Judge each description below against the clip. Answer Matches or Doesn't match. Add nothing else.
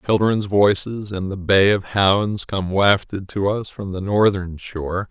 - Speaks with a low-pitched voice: Matches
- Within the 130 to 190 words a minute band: Matches